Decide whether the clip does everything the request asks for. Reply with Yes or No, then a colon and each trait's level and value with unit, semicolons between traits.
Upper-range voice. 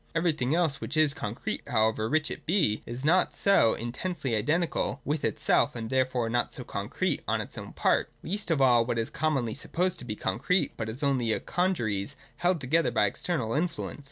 No: low, 135 Hz